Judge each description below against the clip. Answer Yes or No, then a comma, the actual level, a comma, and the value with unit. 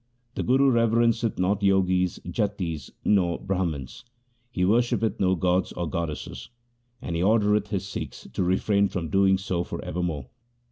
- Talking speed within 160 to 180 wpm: No, average, 150 wpm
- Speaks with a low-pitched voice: Yes, very low, 95 Hz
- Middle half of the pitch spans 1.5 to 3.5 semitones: Yes, average, 3.0 semitones